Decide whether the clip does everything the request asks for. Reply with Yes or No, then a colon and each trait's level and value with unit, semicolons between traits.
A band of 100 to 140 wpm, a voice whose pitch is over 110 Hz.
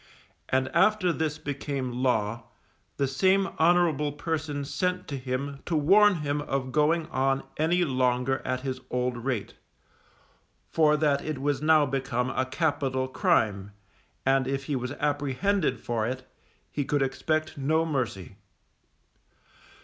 Yes: slow, 135 wpm; medium, 140 Hz